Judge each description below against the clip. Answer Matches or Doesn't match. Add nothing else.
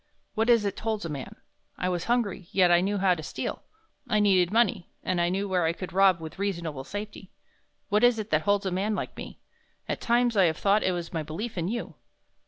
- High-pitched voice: Matches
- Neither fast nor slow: Doesn't match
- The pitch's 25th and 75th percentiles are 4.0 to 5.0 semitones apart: Doesn't match